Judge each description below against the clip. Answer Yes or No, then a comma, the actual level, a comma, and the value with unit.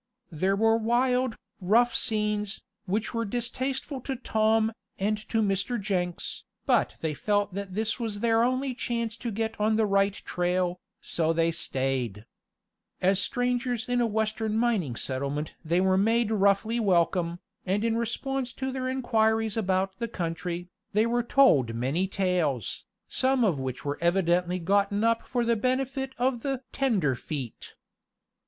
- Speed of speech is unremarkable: Yes, average, 150 wpm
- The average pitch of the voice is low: No, high, 215 Hz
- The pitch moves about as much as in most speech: Yes, average, 4.7 semitones